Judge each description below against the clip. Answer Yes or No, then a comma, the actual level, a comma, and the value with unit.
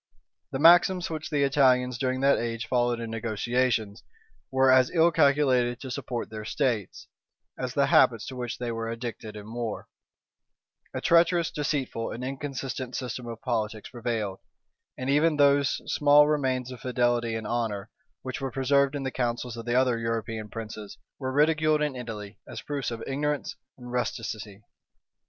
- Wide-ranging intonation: No, average, 3.4 semitones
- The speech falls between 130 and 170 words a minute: Yes, average, 160 wpm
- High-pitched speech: No, low, 125 Hz